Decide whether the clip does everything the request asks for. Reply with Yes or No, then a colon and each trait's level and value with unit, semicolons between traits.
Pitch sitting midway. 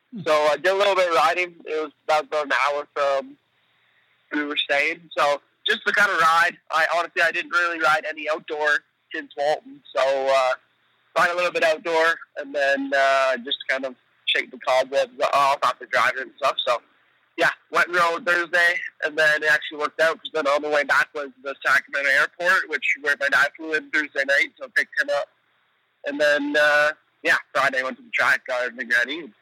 Yes: medium, 150 Hz